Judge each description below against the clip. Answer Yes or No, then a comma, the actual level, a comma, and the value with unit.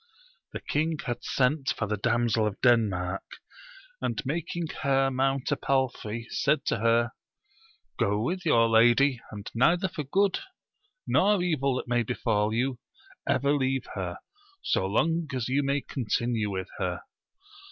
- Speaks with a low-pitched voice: Yes, low, 125 Hz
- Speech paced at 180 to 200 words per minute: No, average, 145 wpm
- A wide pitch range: No, average, 4.1 semitones